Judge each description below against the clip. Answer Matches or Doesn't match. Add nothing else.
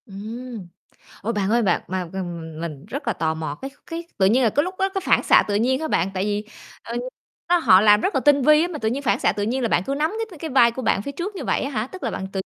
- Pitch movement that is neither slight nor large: Doesn't match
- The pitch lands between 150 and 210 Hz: Doesn't match